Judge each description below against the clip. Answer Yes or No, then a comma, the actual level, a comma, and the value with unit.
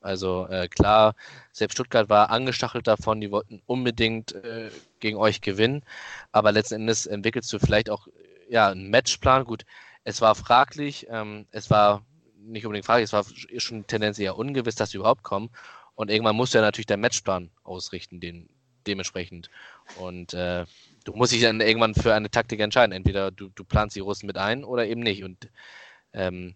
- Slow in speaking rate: No, average, 180 wpm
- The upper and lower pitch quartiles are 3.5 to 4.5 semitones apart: No, average, 2.7 semitones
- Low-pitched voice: Yes, low, 105 Hz